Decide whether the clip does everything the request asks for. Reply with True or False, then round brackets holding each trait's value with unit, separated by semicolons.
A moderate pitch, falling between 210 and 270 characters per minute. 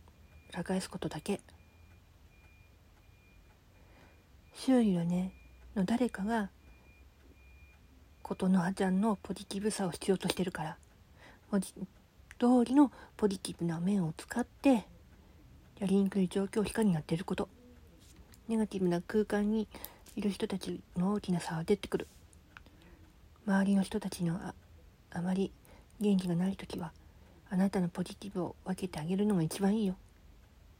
True (180 Hz; 260 characters per minute)